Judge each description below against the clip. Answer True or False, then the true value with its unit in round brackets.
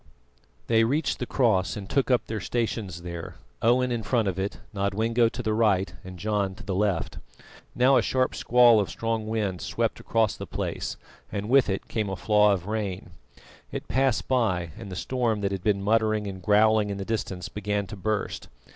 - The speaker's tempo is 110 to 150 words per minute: False (195 wpm)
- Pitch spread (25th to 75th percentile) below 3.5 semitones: True (2.7 semitones)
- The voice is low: True (105 Hz)